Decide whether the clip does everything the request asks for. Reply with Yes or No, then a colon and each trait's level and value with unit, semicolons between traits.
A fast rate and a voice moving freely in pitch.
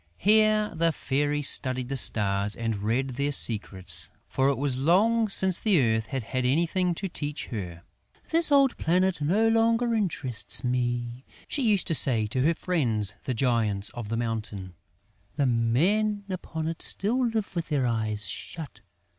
No: average, 165 wpm; wide, 8.5 semitones